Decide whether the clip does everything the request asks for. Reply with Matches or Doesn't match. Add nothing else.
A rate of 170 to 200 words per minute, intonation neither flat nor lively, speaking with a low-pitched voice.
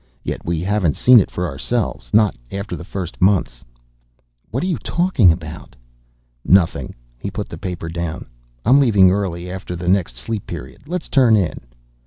Matches